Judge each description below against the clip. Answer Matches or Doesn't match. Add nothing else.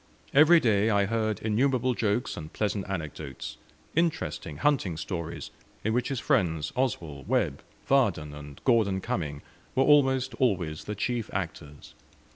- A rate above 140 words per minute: Doesn't match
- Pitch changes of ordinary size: Doesn't match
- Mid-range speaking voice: Doesn't match